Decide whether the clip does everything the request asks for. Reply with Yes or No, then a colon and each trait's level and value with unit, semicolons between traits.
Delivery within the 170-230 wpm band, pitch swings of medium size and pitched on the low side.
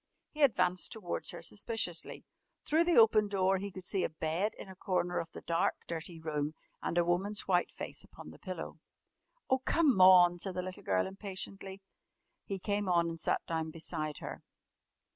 No: average, 180 wpm; average, 3.2 semitones; medium, 185 Hz